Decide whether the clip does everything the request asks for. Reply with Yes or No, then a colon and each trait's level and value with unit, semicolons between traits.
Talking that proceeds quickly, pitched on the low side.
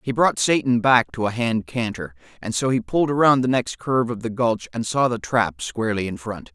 Yes: fast, 240 wpm; low, 115 Hz